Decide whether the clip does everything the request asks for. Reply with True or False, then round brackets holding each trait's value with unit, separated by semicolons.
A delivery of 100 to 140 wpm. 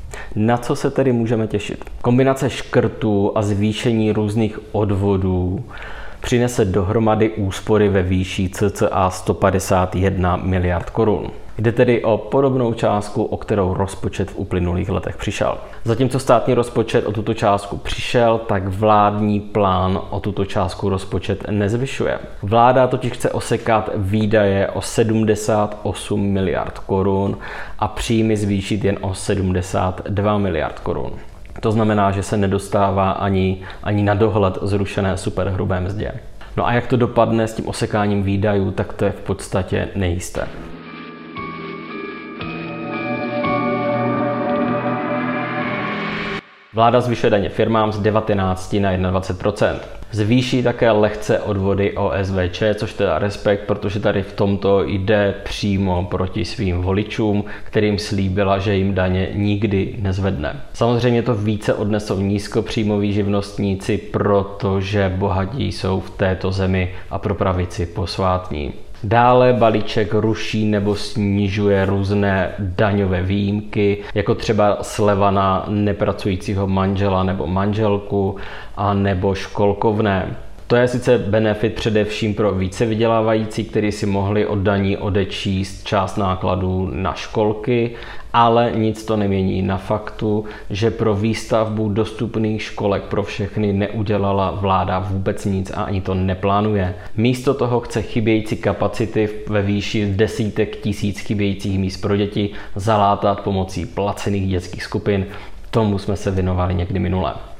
True (125 wpm)